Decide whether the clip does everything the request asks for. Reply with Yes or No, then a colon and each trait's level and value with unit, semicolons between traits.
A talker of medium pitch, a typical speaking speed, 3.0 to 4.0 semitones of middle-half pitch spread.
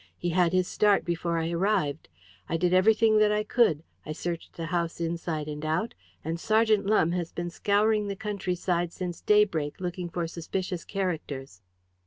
Yes: medium, 175 Hz; average, 175 wpm; average, 3.5 semitones